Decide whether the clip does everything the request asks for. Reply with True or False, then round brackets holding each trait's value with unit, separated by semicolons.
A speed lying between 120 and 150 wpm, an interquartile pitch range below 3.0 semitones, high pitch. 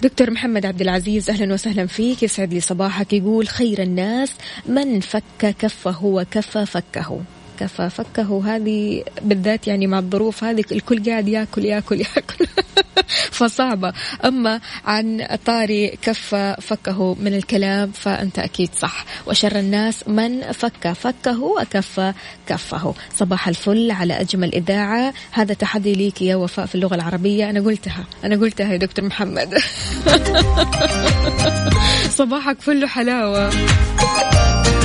True (125 wpm; 2.6 semitones; 210 Hz)